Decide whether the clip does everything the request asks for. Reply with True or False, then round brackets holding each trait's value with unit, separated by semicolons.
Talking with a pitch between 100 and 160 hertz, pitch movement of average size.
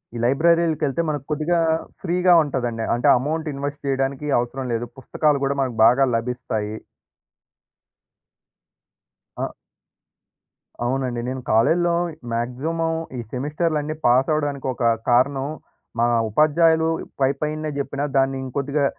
True (140 Hz; 3.5 semitones)